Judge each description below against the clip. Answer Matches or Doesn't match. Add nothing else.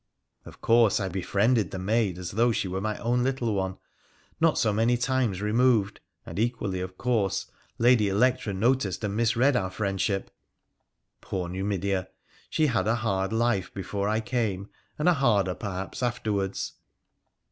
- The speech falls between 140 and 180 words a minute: Matches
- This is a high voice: Doesn't match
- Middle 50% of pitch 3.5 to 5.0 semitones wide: Matches